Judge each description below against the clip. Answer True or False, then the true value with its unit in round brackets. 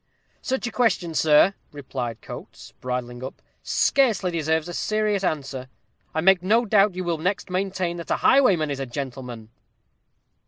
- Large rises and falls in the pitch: True (6.4 semitones)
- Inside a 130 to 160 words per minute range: True (155 wpm)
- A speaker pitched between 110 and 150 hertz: False (170 Hz)